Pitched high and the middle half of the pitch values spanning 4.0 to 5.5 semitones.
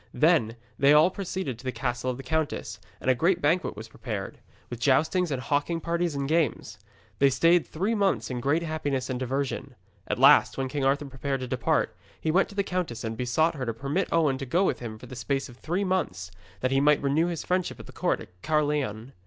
No: medium, 140 Hz; average, 4.8 semitones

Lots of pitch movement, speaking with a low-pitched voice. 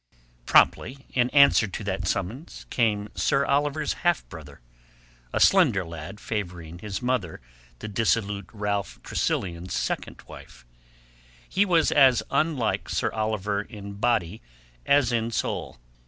Yes: wide, 5.9 semitones; low, 105 Hz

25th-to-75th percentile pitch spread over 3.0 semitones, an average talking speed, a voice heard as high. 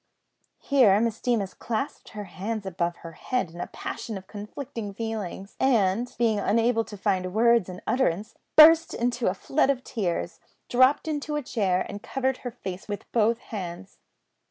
Yes: average, 4.3 semitones; average, 165 wpm; high, 220 Hz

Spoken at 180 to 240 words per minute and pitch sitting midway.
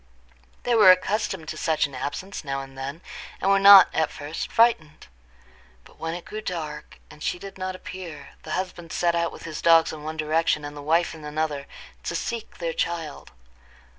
Yes: average, 195 wpm; medium, 165 Hz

